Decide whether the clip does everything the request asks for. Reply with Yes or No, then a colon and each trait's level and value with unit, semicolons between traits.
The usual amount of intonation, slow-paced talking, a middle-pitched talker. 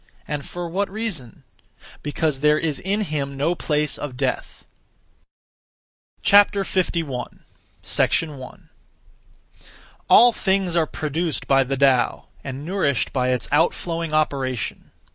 Yes: average, 4.4 semitones; slow, 110 wpm; medium, 150 Hz